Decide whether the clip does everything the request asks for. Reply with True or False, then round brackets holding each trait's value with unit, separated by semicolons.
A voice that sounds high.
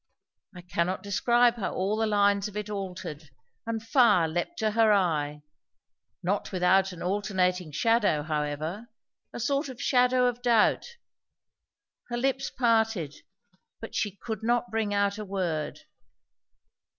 True (205 Hz)